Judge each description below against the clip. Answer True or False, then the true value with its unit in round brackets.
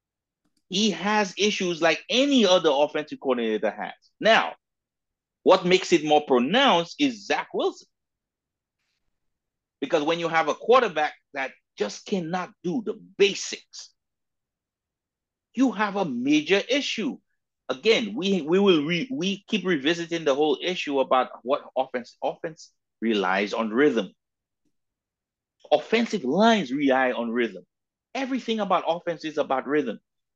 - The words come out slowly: True (125 wpm)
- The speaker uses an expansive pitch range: True (6.7 semitones)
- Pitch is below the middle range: False (185 Hz)